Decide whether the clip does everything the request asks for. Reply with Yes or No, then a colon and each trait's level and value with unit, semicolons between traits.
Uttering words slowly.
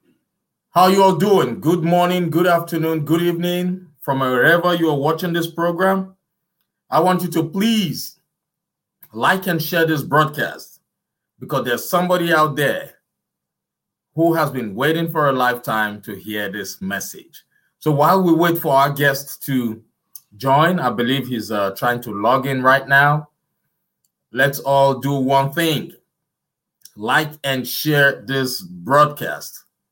No: average, 145 wpm